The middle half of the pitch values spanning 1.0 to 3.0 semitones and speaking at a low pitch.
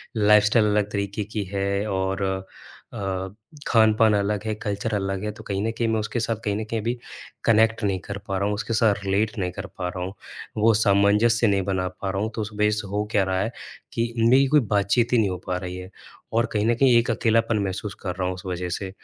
Yes: narrow, 2.4 semitones; low, 105 Hz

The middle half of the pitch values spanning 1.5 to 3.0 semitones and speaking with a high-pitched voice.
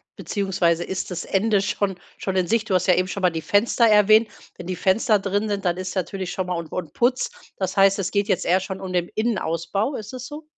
Yes: narrow, 2.5 semitones; high, 195 Hz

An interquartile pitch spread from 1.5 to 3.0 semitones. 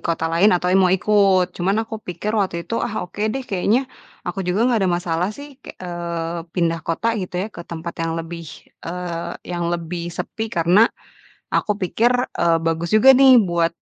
No: average, 3.7 semitones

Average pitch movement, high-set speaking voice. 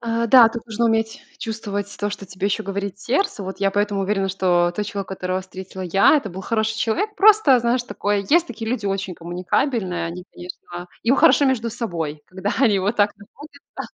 Yes: average, 3.6 semitones; high, 205 Hz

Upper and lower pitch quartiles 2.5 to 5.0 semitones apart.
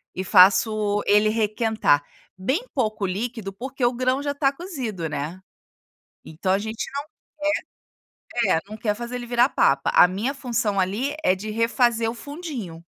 Yes: average, 4.2 semitones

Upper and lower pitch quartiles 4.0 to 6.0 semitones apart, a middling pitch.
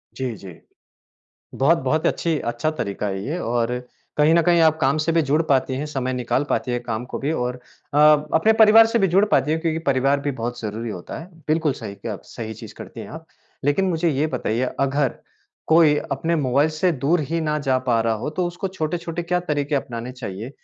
Yes: average, 4.7 semitones; medium, 145 Hz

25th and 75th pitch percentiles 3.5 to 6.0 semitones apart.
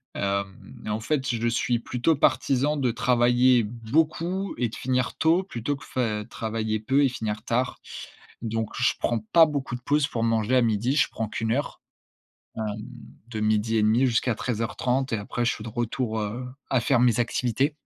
No: average, 2.9 semitones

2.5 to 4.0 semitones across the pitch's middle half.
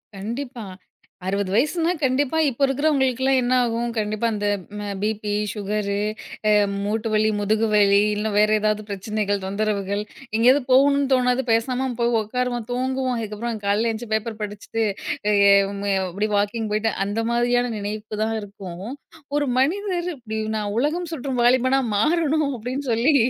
Yes: average, 3.7 semitones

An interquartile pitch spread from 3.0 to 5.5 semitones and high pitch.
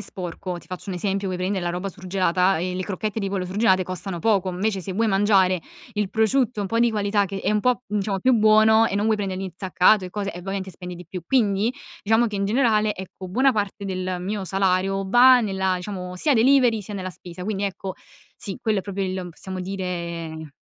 No: narrow, 2.5 semitones; high, 195 Hz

